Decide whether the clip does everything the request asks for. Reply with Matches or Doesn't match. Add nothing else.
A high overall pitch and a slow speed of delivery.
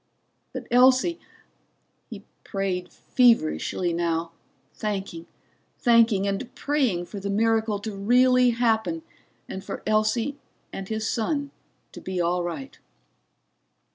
Matches